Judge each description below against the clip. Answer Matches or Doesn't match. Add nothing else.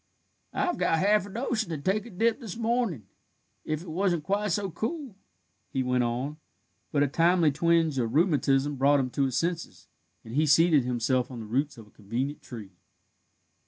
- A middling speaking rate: Matches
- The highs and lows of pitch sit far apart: Matches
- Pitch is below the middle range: Doesn't match